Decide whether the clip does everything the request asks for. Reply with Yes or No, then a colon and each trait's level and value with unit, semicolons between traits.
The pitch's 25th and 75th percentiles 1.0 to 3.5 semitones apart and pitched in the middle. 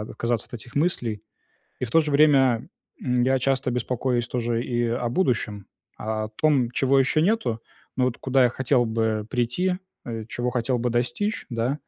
No: narrow, 2.4 semitones; low, 125 Hz